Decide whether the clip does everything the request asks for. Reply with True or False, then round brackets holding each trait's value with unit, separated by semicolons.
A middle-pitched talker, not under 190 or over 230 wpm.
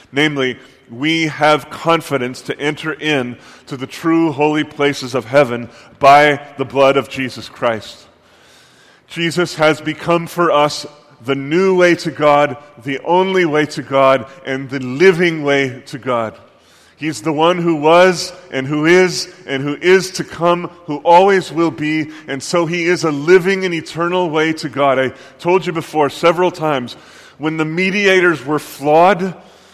False (155 Hz; 160 wpm)